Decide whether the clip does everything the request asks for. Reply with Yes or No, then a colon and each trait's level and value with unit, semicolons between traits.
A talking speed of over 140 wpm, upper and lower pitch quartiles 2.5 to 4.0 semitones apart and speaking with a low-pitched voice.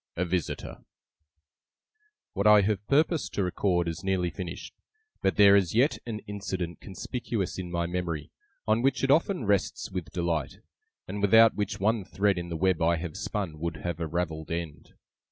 Yes: average, 170 wpm; average, 3.4 semitones; very low, 95 Hz